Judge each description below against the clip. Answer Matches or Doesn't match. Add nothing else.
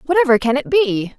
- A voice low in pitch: Doesn't match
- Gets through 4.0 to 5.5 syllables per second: Doesn't match